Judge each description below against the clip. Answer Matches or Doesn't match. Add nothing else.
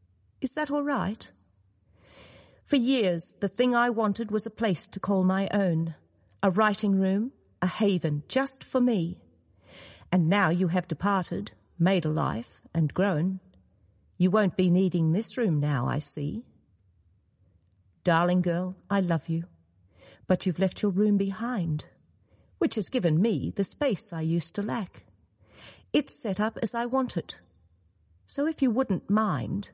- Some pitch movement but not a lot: Doesn't match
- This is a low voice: Doesn't match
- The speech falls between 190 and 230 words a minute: Doesn't match